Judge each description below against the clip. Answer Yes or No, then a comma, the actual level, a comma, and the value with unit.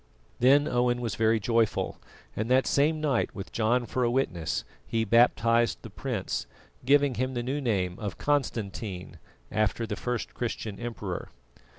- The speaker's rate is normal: Yes, average, 155 wpm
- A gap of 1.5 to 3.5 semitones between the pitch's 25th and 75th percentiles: Yes, average, 3.0 semitones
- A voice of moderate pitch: No, low, 115 Hz